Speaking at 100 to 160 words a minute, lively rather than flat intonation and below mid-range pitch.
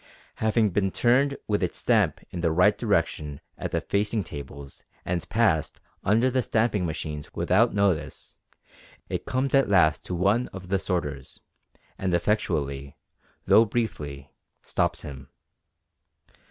Yes: slow, 135 wpm; wide, 6.1 semitones; very low, 95 Hz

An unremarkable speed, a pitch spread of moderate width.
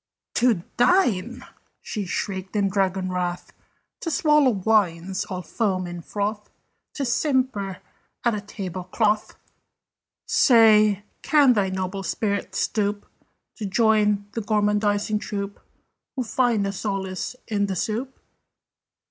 No: slow, 120 wpm; average, 3.1 semitones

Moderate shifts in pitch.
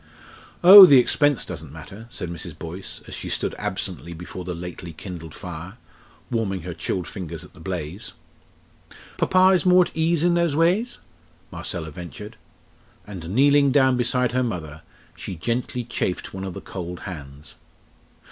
No: wide, 7.4 semitones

